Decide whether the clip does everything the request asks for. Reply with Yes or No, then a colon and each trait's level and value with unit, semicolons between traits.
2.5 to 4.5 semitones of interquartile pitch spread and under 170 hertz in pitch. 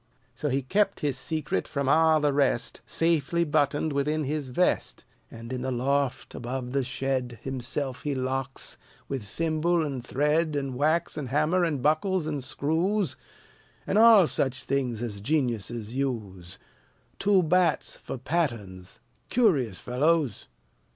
Yes: average, 4.0 semitones; medium, 140 Hz